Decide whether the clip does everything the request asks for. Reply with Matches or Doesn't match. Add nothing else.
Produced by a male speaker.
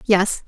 Doesn't match